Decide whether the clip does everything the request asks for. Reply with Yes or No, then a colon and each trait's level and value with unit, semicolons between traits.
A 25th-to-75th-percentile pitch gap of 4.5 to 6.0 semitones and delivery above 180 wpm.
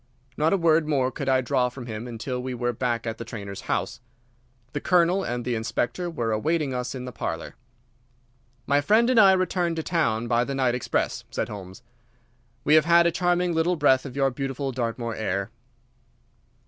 Yes: wide, 5.5 semitones; average, 190 wpm